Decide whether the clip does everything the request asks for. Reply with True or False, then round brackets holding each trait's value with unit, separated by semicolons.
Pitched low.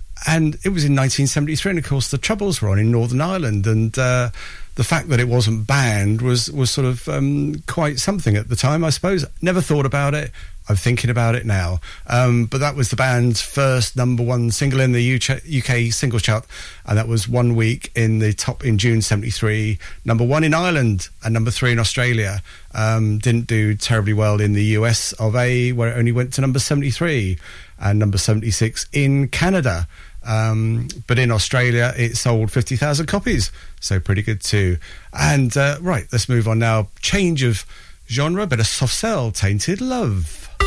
True (120 Hz)